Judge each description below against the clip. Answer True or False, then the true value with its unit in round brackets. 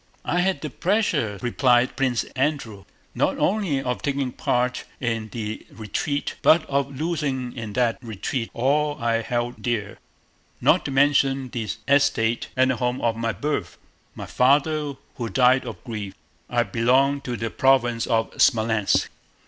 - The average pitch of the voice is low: True (125 Hz)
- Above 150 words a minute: False (140 wpm)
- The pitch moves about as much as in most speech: True (3.4 semitones)